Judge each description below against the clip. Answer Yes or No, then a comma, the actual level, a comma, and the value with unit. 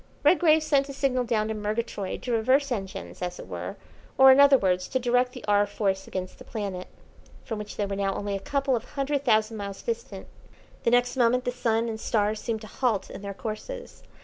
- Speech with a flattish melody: No, average, 4.2 semitones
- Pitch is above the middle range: Yes, high, 225 Hz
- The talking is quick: Yes, fast, 215 wpm